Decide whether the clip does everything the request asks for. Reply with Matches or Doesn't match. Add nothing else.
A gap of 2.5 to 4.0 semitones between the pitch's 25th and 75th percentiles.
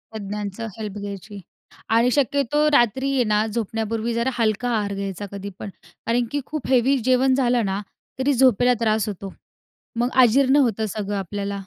Matches